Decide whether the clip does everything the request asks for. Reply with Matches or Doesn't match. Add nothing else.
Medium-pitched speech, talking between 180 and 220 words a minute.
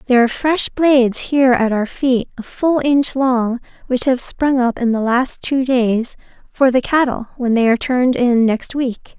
Doesn't match